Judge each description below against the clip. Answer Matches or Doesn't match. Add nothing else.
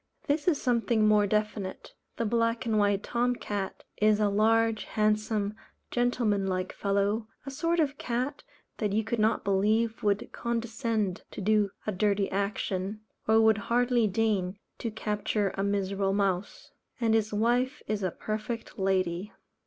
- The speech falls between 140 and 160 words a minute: Matches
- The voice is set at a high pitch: Matches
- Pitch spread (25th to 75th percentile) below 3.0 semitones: Matches